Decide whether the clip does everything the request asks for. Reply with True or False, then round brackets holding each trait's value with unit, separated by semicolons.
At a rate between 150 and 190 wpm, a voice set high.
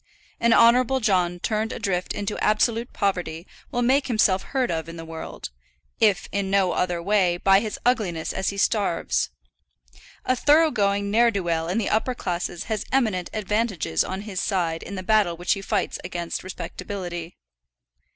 True (170 wpm; 195 Hz)